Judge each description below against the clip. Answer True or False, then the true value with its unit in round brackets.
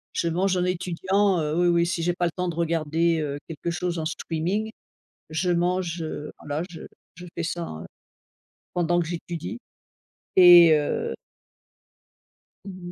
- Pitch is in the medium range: True (170 Hz)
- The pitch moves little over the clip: True (1.7 semitones)